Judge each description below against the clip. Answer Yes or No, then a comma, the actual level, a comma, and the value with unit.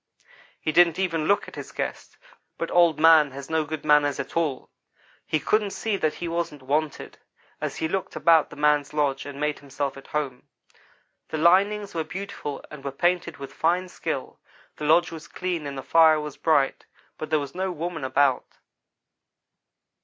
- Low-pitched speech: No, medium, 155 Hz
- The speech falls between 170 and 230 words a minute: Yes, average, 180 wpm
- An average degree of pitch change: Yes, average, 3.1 semitones